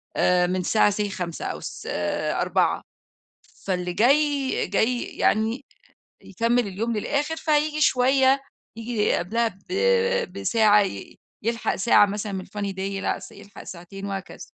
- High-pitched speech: Yes, high, 215 Hz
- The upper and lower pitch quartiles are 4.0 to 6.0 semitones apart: Yes, average, 4.3 semitones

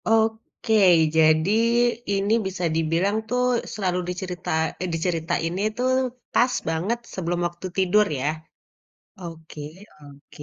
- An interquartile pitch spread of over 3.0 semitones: Yes, average, 3.9 semitones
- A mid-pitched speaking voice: Yes, medium, 180 Hz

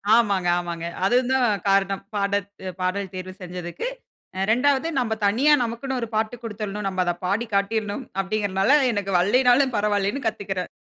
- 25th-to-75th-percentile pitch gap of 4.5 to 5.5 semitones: No, average, 3.7 semitones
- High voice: Yes, high, 205 Hz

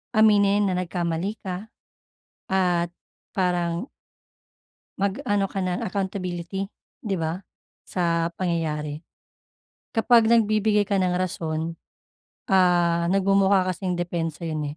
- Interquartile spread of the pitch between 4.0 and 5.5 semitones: No, average, 2.7 semitones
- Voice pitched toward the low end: No, medium, 185 Hz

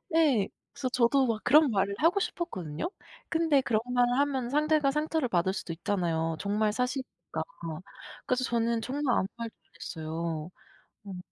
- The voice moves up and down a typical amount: No, wide, 6.8 semitones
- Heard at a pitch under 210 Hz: No, high, 235 Hz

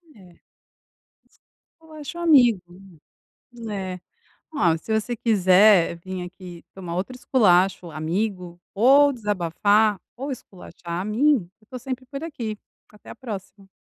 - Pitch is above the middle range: Yes, high, 205 Hz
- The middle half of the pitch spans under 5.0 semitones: No, wide, 5.5 semitones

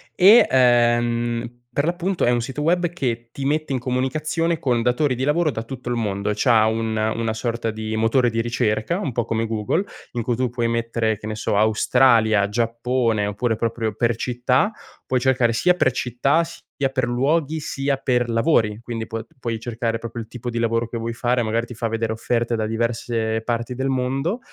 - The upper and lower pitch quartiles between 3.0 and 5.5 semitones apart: No, narrow, 2.5 semitones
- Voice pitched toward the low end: Yes, low, 120 Hz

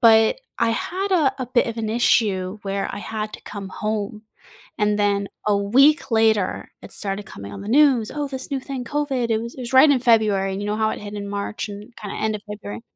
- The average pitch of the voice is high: Yes, high, 220 Hz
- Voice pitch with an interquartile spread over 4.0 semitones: No, average, 3.7 semitones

